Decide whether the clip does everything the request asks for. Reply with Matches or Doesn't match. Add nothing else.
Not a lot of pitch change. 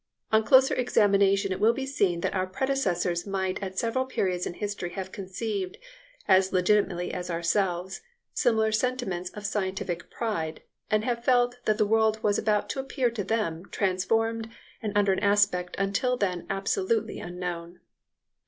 Doesn't match